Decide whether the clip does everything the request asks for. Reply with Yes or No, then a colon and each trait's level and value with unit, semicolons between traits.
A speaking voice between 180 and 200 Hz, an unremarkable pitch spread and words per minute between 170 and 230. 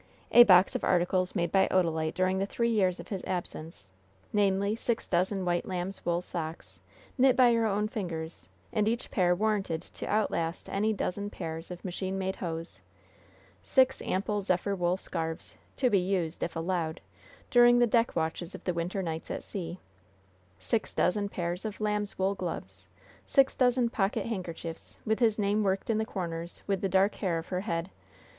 Yes: high, 190 Hz; average, 3.4 semitones; average, 180 wpm